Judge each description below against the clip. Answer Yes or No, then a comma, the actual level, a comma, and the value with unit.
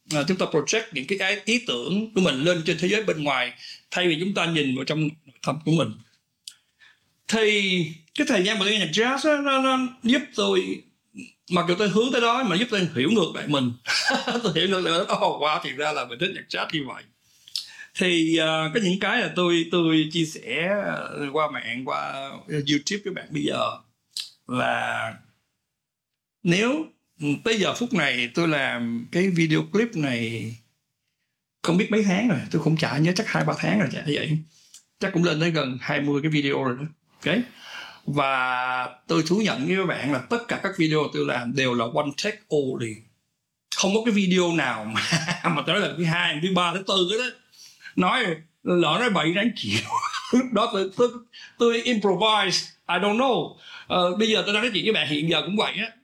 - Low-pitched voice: No, medium, 175 Hz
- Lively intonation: Yes, wide, 5.9 semitones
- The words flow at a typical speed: Yes, average, 200 wpm